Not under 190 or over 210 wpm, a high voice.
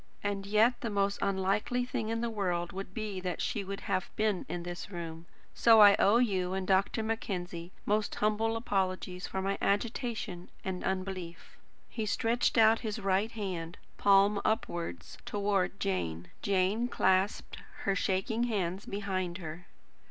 No: average, 150 wpm; high, 195 Hz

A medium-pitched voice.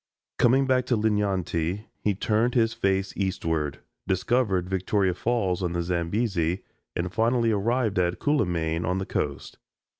No: very low, 95 Hz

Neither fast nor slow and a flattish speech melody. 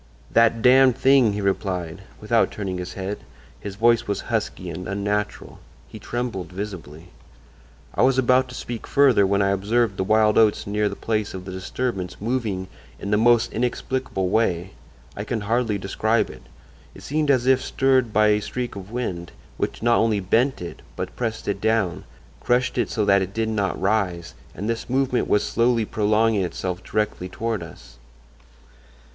No: average, 170 wpm; average, 3.5 semitones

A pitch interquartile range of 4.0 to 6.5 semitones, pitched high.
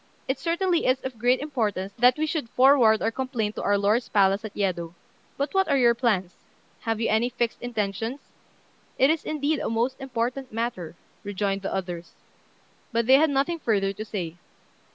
Yes: average, 4.7 semitones; high, 235 Hz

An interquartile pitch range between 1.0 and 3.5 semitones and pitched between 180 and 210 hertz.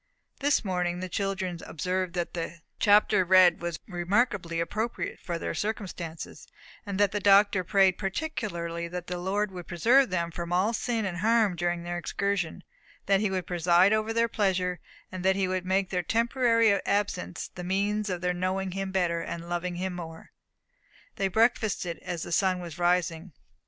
Yes: narrow, 2.6 semitones; medium, 185 Hz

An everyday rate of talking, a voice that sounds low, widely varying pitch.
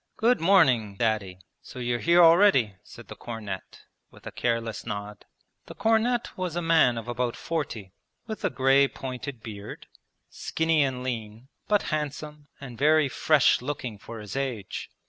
Yes: average, 155 wpm; low, 130 Hz; wide, 5.9 semitones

